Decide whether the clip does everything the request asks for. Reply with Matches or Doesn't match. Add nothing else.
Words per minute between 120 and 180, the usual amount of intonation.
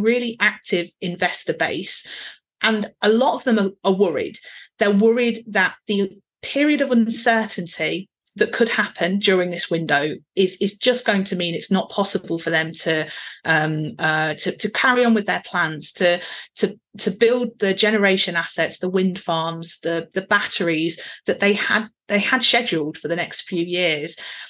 Matches